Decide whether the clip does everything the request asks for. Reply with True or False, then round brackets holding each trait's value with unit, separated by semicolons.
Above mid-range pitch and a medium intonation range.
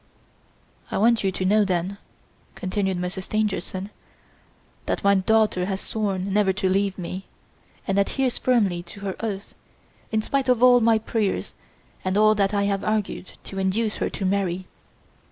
False (200 Hz; 2.3 semitones)